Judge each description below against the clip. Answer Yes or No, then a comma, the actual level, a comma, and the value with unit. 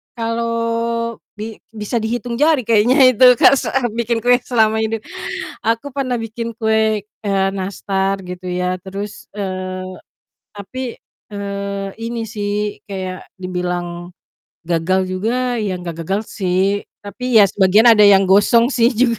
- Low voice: No, high, 210 Hz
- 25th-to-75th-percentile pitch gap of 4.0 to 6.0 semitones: No, average, 3.3 semitones